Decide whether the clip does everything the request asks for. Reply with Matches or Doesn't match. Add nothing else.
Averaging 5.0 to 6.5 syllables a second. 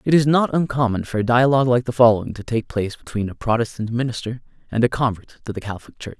Doesn't match